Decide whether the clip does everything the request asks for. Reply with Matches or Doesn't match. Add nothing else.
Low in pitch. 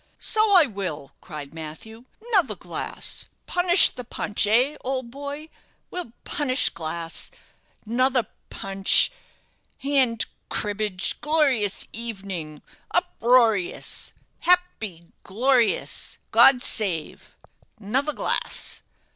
Doesn't match